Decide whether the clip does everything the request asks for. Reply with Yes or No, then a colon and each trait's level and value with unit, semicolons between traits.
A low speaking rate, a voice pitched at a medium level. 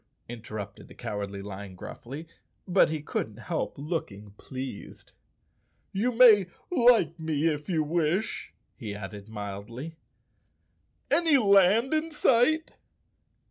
Yes: slow, 110 wpm; medium, 155 Hz